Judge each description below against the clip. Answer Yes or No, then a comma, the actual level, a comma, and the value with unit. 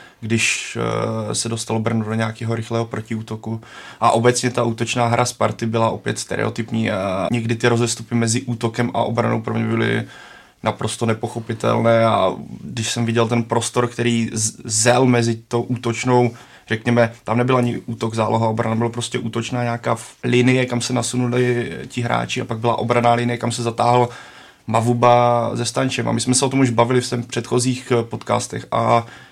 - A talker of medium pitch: No, low, 120 Hz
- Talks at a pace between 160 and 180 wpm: Yes, fast, 170 wpm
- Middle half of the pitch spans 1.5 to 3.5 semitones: No, narrow, 1.1 semitones